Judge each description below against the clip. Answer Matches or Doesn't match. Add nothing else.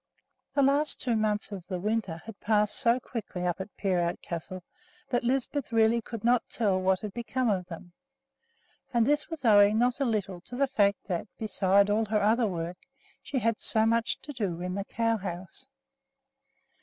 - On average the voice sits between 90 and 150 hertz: Doesn't match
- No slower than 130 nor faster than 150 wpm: Doesn't match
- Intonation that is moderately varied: Matches